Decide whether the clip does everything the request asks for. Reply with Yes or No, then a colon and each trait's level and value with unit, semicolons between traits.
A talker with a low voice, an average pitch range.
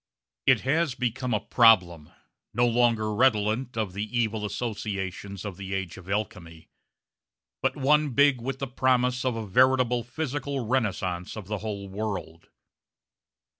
Yes: low, 110 Hz; average, 4.3 semitones